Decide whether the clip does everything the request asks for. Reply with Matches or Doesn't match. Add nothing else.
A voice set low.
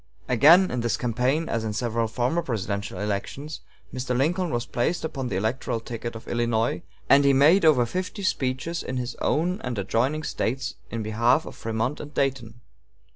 Matches